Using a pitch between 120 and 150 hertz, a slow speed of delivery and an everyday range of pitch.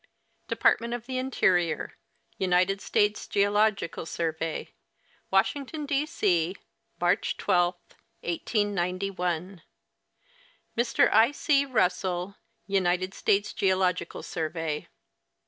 No: high, 190 Hz; slow, 85 wpm; average, 3.5 semitones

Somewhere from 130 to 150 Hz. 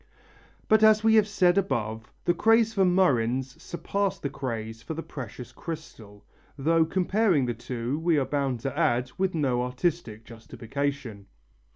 Yes: medium, 140 Hz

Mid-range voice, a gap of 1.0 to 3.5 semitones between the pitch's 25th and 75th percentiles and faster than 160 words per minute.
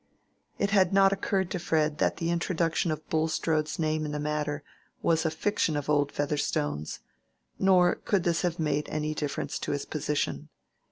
Yes: medium, 160 Hz; average, 2.8 semitones; average, 170 wpm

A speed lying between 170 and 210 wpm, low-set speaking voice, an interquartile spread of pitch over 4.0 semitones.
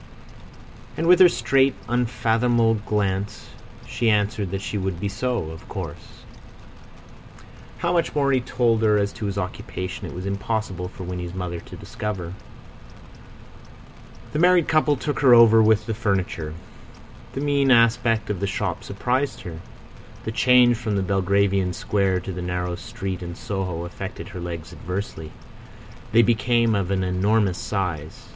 No: average, 150 wpm; low, 105 Hz; average, 4.4 semitones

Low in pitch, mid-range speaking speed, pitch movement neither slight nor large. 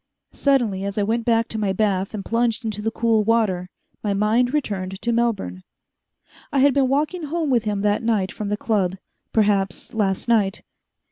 No: high, 215 Hz; average, 185 wpm; average, 3.0 semitones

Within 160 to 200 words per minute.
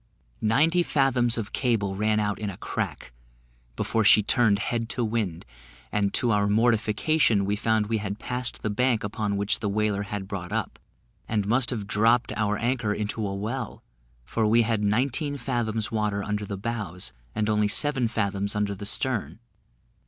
Yes: average, 175 wpm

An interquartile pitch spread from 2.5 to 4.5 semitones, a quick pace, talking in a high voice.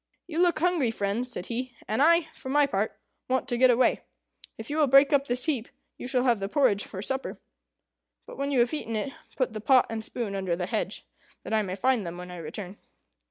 No: average, 5.0 semitones; fast, 230 wpm; high, 245 Hz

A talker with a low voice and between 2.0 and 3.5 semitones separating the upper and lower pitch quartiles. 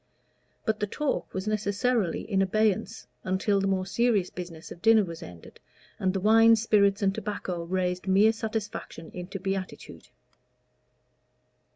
No: high, 195 Hz; narrow, 2.6 semitones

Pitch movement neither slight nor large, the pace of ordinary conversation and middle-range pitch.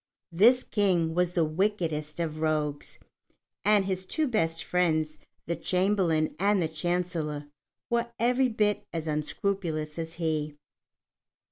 No: average, 4.2 semitones; slow, 125 wpm; medium, 170 Hz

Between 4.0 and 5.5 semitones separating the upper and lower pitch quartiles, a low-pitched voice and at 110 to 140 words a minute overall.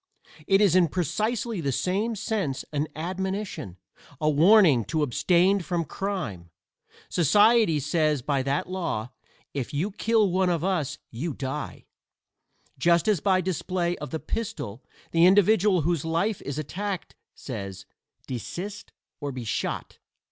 No: average, 5.2 semitones; medium, 170 Hz; slow, 135 wpm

